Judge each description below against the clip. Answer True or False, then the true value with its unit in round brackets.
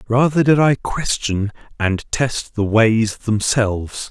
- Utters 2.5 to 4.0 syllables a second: True (3.6 syllables/s)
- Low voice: True (115 Hz)